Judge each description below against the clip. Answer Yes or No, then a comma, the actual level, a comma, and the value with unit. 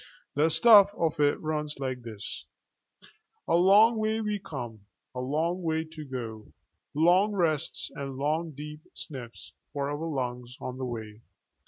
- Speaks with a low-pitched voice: No, medium, 150 Hz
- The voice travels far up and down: No, average, 4.7 semitones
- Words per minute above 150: No, average, 145 wpm